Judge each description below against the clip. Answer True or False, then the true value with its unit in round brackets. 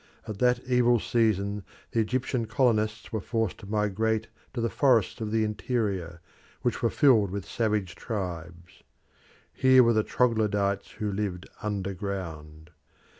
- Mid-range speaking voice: False (105 Hz)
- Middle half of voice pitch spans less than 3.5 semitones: True (3.0 semitones)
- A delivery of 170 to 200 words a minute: False (140 wpm)